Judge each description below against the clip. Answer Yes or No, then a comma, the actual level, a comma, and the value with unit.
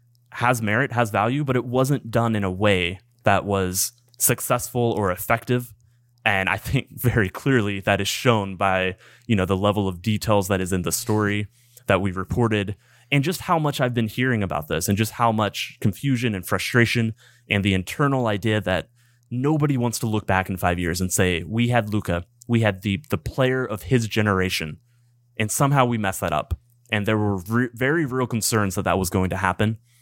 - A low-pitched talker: Yes, low, 110 Hz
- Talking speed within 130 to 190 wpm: No, average, 200 wpm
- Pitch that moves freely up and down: No, average, 3.7 semitones